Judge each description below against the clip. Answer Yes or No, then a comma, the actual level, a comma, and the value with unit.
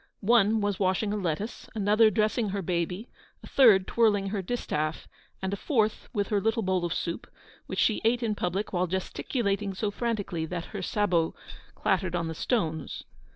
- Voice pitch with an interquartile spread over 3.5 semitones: No, average, 3.2 semitones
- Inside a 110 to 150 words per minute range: No, average, 175 wpm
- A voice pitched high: Yes, high, 200 Hz